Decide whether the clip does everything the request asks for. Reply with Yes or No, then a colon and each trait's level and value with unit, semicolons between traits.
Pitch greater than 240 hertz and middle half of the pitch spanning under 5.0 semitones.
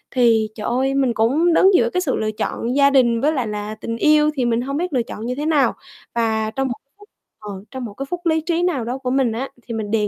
Yes: very high, 255 Hz; average, 4.4 semitones